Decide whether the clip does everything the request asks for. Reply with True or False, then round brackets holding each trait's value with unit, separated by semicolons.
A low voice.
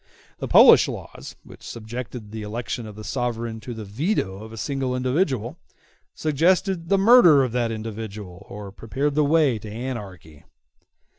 True (120 Hz)